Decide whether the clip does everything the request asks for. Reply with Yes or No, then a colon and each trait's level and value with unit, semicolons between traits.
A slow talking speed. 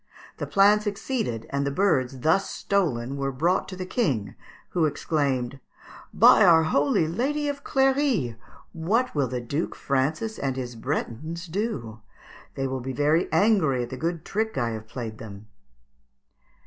No: average, 155 wpm